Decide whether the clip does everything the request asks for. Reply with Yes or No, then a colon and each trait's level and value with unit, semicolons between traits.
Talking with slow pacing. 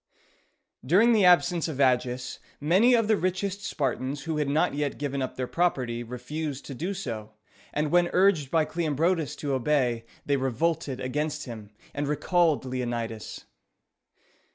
No: average, 150 wpm